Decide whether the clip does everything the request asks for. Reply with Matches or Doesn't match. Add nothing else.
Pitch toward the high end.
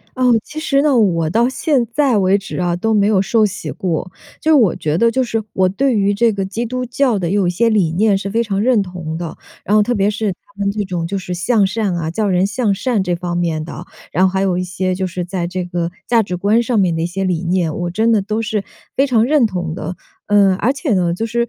Matches